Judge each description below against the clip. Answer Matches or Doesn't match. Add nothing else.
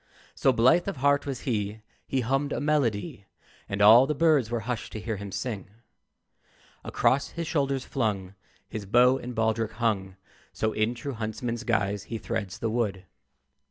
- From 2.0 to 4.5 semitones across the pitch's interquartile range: Matches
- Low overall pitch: Matches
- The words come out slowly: Doesn't match